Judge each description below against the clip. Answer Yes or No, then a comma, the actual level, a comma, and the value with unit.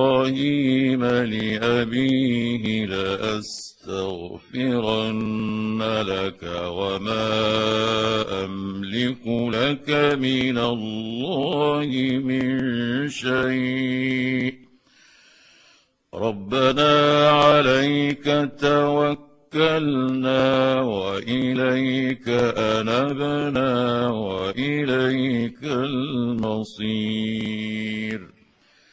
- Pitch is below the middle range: Yes, low, 125 Hz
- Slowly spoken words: Yes, slow, 35 wpm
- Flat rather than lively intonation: No, average, 3.2 semitones